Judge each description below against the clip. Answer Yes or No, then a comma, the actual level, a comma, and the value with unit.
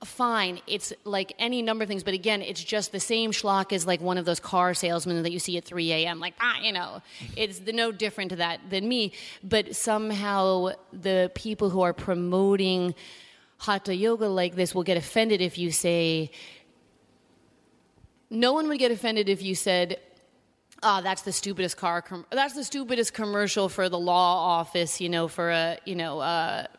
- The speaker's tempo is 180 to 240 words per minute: Yes, average, 195 wpm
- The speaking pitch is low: No, high, 190 Hz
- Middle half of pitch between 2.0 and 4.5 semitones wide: Yes, average, 3.3 semitones